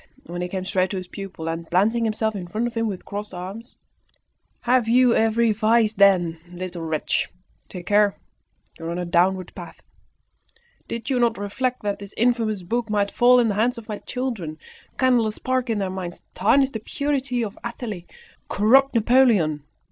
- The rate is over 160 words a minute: Yes, average, 185 wpm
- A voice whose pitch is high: Yes, high, 215 Hz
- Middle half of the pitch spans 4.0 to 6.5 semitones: Yes, average, 4.3 semitones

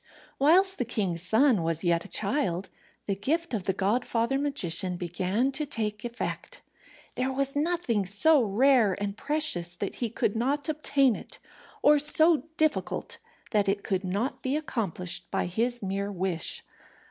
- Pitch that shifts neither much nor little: No, wide, 6.6 semitones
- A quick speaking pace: No, average, 155 wpm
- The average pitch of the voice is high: Yes, high, 225 Hz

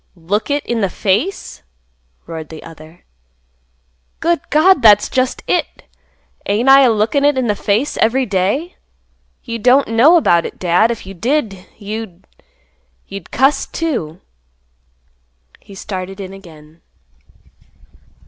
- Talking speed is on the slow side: Yes, slow, 130 wpm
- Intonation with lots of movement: Yes, wide, 6.4 semitones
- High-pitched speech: Yes, high, 210 Hz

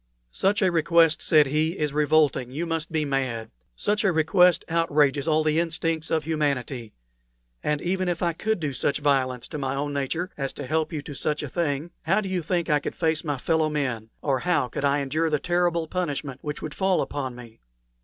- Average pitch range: Yes, average, 3.1 semitones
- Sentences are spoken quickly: Yes, fast, 210 wpm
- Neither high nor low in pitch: Yes, medium, 155 Hz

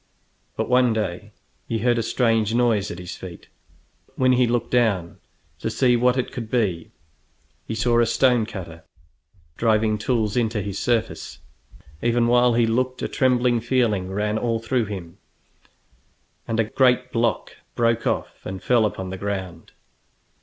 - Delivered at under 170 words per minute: Yes, average, 160 wpm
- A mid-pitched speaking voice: No, low, 115 Hz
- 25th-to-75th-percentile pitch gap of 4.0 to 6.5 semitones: No, average, 2.9 semitones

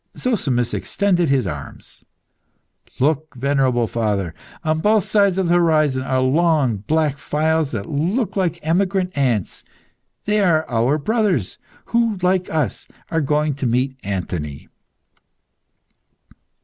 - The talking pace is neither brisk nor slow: No, slow, 125 wpm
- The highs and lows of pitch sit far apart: Yes, wide, 5.9 semitones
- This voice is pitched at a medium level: Yes, medium, 150 Hz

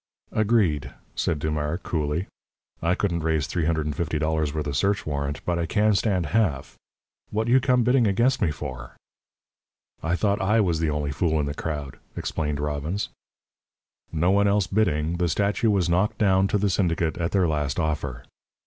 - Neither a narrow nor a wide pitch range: Yes, average, 5.0 semitones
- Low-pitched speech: Yes, very low, 85 Hz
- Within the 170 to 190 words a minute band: Yes, average, 180 wpm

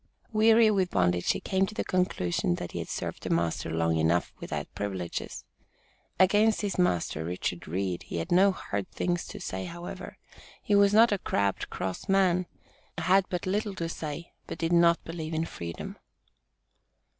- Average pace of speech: Yes, average, 170 wpm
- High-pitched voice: No, medium, 170 Hz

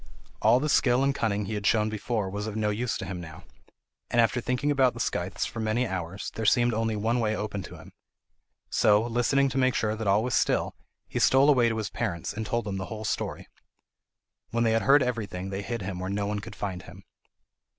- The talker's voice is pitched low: Yes, low, 110 Hz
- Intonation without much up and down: No, average, 3.0 semitones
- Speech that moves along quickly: Yes, fast, 230 wpm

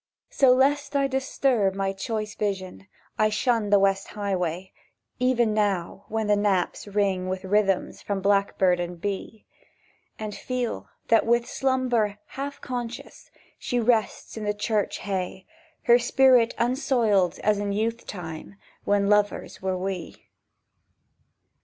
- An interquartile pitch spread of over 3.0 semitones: Yes, average, 3.5 semitones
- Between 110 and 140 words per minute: Yes, slow, 135 wpm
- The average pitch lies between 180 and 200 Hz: No, high, 210 Hz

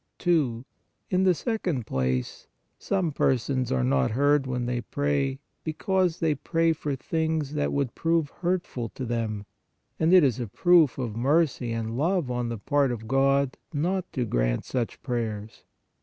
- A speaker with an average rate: Yes, average, 170 wpm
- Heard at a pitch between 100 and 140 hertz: Yes, low, 135 Hz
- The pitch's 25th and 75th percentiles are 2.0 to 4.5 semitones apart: No, wide, 5.5 semitones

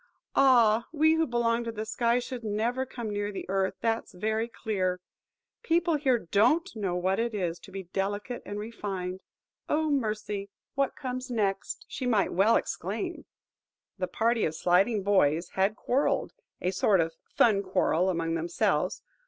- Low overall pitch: No, high, 215 Hz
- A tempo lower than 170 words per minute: Yes, average, 160 wpm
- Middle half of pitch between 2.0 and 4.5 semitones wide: Yes, average, 4.0 semitones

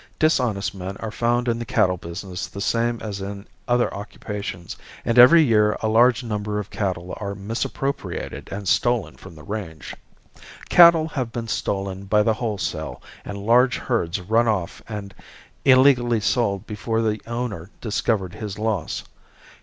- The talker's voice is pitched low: Yes, low, 105 Hz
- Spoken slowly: No, average, 155 wpm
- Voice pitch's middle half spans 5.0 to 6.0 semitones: No, average, 3.2 semitones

